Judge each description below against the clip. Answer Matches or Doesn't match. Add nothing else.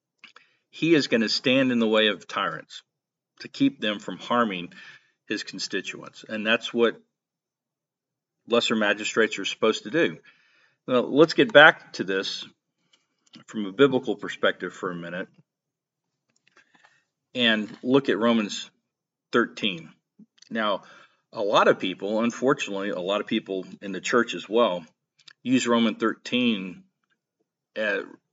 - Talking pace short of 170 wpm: Matches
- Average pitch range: Matches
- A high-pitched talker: Doesn't match